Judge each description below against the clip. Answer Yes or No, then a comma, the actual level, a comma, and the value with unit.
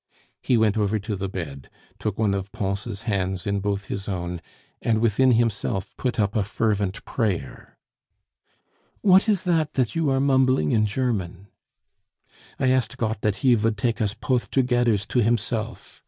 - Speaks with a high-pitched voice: No, low, 110 Hz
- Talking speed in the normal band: Yes, average, 165 wpm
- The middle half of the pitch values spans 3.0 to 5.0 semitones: Yes, average, 3.9 semitones